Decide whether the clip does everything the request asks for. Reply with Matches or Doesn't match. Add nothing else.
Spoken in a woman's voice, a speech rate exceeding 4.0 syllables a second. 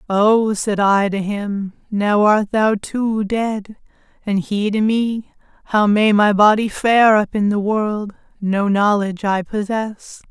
Doesn't match